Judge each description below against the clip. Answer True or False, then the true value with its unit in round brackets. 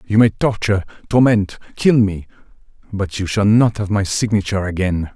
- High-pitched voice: False (100 Hz)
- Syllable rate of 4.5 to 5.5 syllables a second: True (5.3 syllables/s)